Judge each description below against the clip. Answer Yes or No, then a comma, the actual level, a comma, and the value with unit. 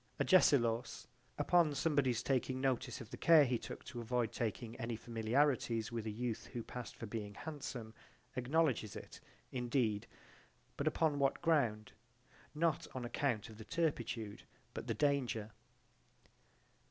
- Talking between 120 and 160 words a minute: Yes, average, 140 wpm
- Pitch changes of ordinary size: Yes, average, 4.1 semitones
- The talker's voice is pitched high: No, low, 125 Hz